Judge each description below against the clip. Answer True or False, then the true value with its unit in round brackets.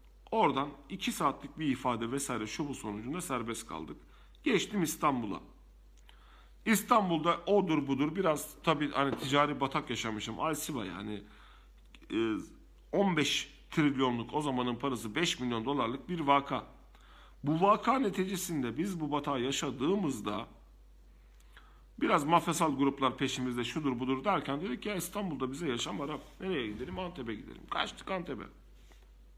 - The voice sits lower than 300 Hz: True (140 Hz)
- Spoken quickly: False (125 wpm)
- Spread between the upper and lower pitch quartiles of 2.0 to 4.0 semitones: False (5.1 semitones)